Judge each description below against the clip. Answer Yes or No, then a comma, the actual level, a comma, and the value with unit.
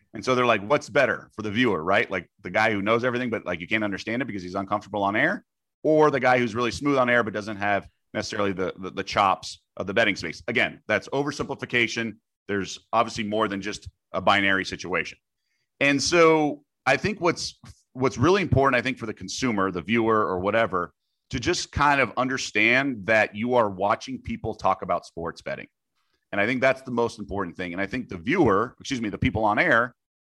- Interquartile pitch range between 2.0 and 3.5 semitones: No, average, 4.2 semitones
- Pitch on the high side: No, low, 110 Hz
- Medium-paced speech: No, fast, 215 wpm